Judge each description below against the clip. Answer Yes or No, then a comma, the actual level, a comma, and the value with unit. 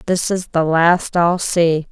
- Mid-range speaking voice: Yes, medium, 170 Hz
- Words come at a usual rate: Yes, average, 190 wpm